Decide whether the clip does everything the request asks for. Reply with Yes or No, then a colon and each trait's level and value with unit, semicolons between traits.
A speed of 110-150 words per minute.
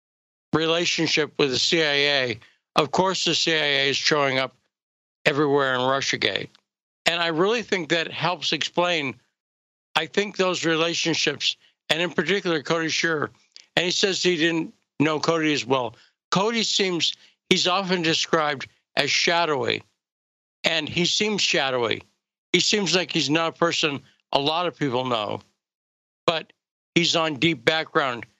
Yes: average, 140 wpm